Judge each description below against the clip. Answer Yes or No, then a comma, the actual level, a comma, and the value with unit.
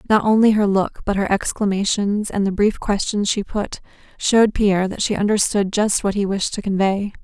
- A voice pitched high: Yes, high, 200 Hz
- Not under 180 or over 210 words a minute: Yes, average, 200 wpm